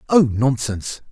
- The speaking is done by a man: Yes, male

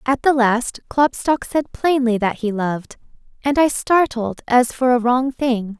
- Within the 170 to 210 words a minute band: Yes, average, 175 wpm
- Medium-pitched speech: No, very high, 250 Hz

